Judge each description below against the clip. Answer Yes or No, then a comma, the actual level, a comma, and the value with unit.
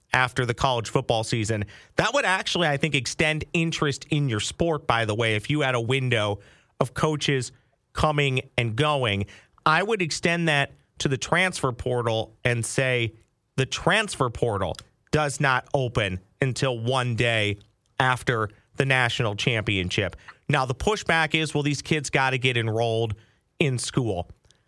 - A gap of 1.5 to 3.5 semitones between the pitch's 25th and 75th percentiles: No, average, 4.5 semitones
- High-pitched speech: No, low, 130 Hz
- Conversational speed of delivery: Yes, average, 155 wpm